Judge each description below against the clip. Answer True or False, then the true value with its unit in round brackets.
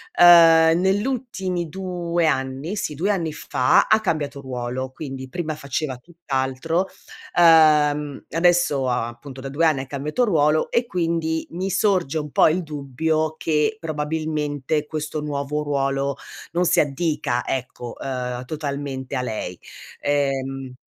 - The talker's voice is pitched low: False (150 Hz)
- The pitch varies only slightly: False (3.6 semitones)